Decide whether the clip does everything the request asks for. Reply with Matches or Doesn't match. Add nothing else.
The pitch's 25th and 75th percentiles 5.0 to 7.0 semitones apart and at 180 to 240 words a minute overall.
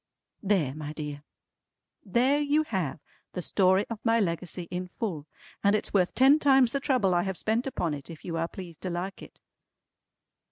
Matches